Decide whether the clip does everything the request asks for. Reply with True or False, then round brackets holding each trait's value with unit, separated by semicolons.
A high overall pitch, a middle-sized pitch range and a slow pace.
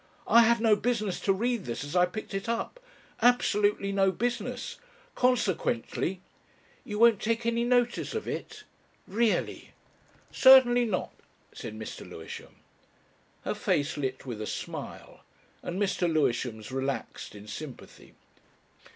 False (205 Hz; 7.9 semitones; 130 wpm)